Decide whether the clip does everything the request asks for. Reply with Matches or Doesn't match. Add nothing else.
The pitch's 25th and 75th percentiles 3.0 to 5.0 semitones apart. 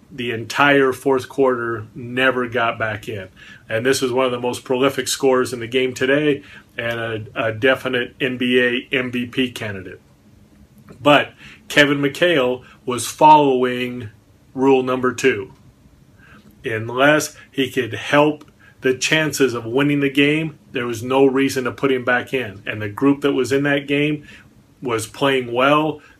Doesn't match